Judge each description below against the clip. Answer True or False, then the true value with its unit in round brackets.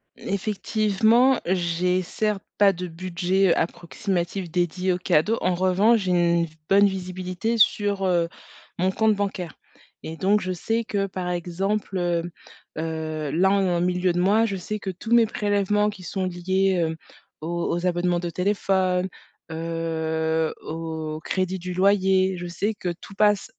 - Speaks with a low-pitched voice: False (185 Hz)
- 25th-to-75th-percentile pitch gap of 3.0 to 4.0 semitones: False (2.5 semitones)